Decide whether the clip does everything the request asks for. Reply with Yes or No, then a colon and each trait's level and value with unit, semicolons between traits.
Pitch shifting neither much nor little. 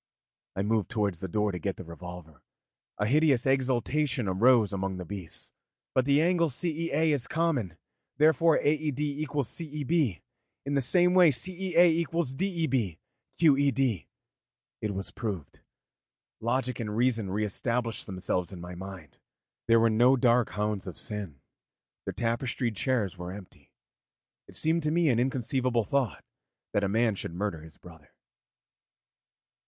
No: wide, 6.8 semitones